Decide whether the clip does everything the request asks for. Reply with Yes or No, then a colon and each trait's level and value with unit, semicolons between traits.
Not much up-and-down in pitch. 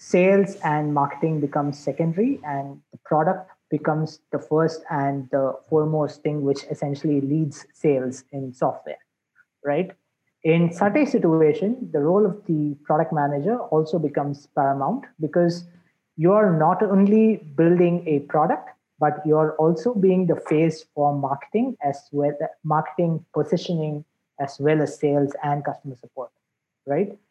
No: average, 3.2 semitones